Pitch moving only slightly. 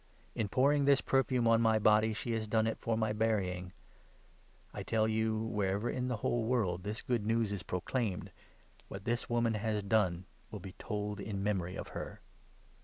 Yes: narrow, 2.3 semitones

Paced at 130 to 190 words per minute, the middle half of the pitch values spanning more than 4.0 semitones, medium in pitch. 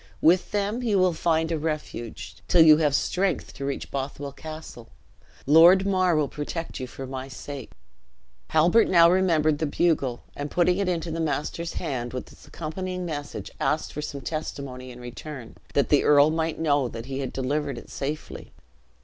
No: average, 175 wpm; average, 3.5 semitones; medium, 155 Hz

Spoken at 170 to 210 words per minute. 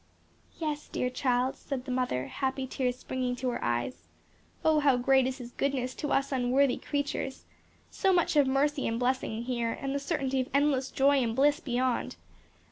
Yes: average, 180 wpm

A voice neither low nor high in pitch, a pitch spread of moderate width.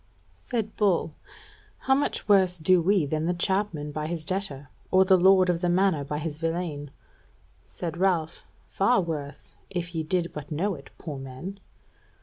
Yes: medium, 175 Hz; average, 3.6 semitones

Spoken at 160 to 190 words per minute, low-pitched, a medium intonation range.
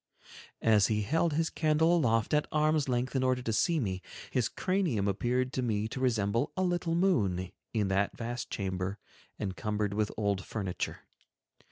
No: average, 165 wpm; low, 115 Hz; wide, 6.8 semitones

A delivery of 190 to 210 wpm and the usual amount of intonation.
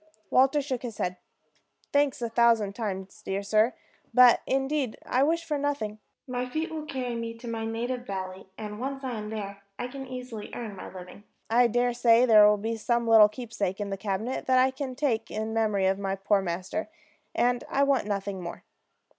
Yes: average, 195 wpm; average, 3.6 semitones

